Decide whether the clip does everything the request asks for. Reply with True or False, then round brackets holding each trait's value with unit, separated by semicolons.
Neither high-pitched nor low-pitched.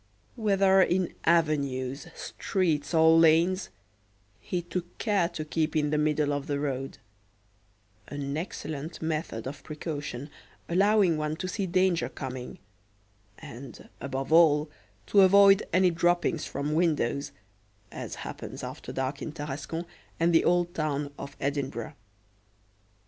True (155 Hz)